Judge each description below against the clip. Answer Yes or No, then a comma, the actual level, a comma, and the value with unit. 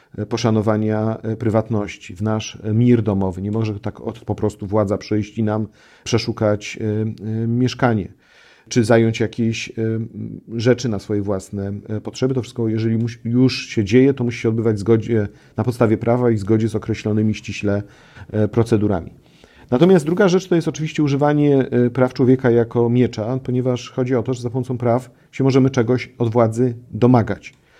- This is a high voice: No, low, 115 Hz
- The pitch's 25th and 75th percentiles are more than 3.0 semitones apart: No, narrow, 2.6 semitones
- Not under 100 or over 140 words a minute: No, average, 150 wpm